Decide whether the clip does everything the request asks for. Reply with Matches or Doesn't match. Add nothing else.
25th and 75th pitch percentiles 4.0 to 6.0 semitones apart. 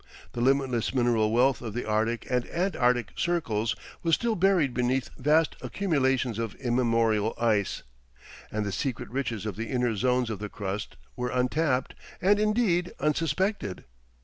Matches